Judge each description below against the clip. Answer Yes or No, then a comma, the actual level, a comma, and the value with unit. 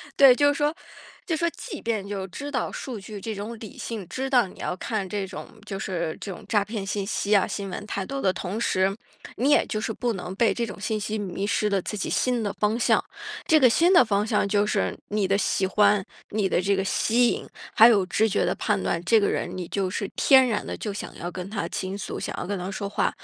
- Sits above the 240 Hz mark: No, high, 205 Hz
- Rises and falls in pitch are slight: No, average, 3.0 semitones